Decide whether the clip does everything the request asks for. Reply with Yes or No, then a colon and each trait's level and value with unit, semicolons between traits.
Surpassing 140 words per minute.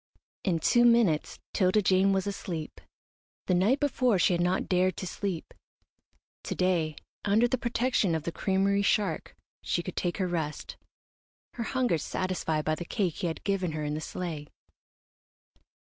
Yes: average, 165 wpm